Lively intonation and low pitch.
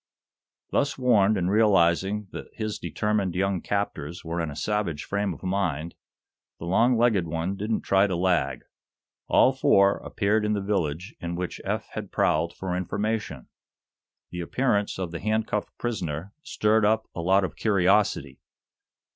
No: average, 3.6 semitones; low, 100 Hz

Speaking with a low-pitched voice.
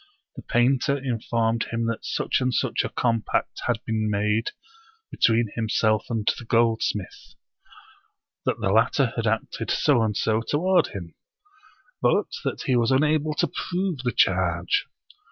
Yes: low, 115 Hz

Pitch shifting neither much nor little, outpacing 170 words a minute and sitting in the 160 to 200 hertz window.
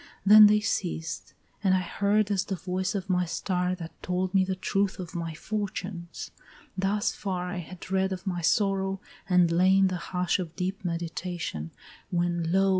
No: narrow, 1.8 semitones; average, 180 wpm; medium, 185 Hz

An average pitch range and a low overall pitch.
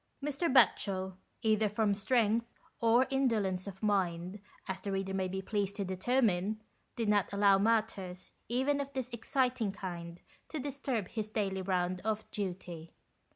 No: average, 3.5 semitones; high, 205 Hz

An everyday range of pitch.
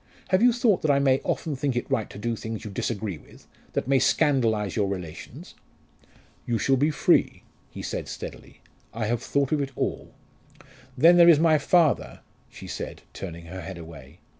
No: wide, 6.7 semitones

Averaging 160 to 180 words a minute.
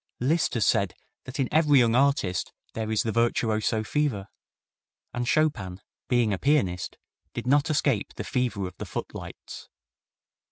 No: average, 150 wpm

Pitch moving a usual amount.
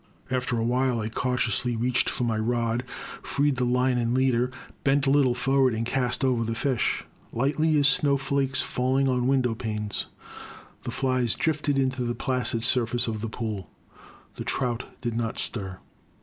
No: narrow, 2.3 semitones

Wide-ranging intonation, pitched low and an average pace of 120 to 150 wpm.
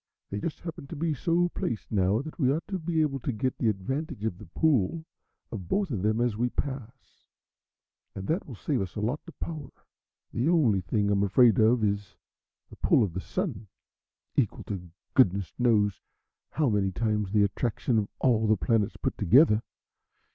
No: wide, 5.8 semitones; low, 115 Hz; average, 190 wpm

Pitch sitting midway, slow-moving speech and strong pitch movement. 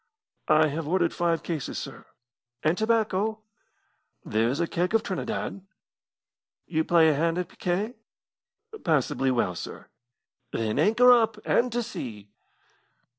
Yes: medium, 170 Hz; slow, 130 wpm; wide, 6.2 semitones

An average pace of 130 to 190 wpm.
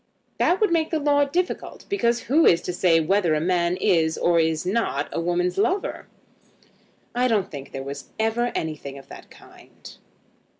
Yes: average, 175 wpm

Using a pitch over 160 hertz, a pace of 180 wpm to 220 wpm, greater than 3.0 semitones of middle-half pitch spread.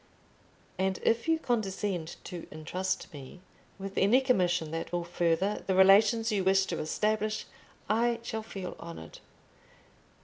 No: high, 190 Hz; slow, 135 wpm; average, 3.7 semitones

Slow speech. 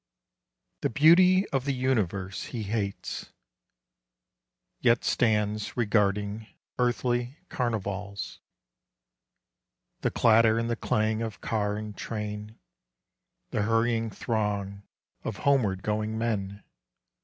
Yes: slow, 100 wpm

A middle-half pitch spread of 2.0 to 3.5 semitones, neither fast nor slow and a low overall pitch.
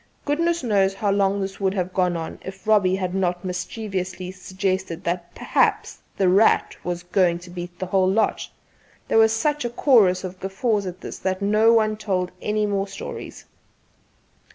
No: narrow, 2.6 semitones; average, 175 wpm; high, 190 Hz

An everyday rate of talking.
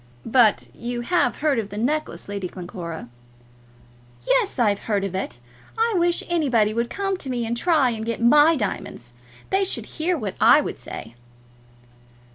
Yes: average, 165 wpm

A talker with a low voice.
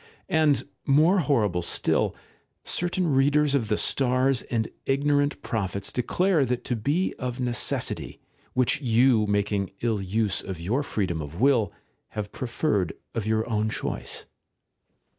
Yes: low, 120 Hz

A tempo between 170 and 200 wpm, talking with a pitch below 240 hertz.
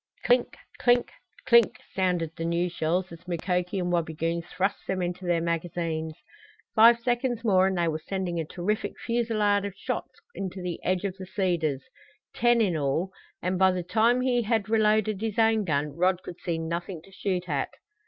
Yes: average, 180 wpm; medium, 185 Hz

